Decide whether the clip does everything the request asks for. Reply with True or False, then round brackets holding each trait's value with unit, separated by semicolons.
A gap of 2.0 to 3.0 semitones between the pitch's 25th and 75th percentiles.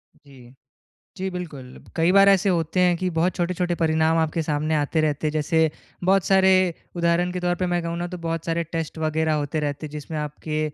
True (2.5 semitones)